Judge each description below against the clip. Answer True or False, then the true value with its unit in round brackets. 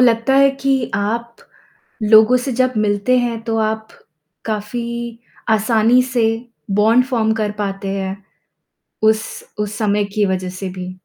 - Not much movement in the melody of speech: True (2.3 semitones)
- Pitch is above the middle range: True (220 Hz)